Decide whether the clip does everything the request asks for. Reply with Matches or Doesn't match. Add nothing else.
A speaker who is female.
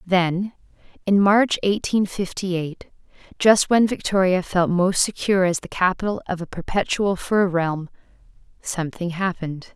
Matches